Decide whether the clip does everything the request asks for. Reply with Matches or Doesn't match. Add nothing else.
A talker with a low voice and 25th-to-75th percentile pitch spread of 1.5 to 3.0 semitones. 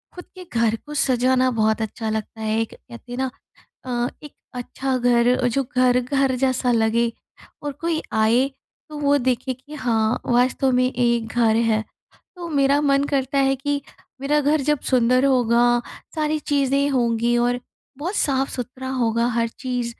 Doesn't match